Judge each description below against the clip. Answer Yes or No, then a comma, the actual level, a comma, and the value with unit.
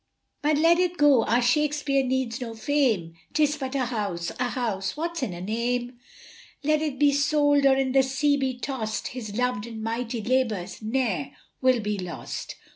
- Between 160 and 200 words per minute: Yes, average, 180 wpm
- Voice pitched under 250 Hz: No, very high, 255 Hz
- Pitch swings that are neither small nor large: Yes, average, 4.2 semitones